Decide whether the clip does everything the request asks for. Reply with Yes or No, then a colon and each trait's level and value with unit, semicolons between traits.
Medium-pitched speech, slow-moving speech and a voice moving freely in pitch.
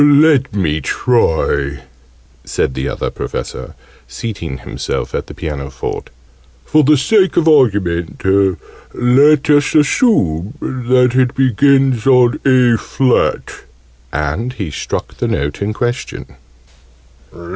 No: low, 125 Hz; slow, 115 wpm; wide, 8.6 semitones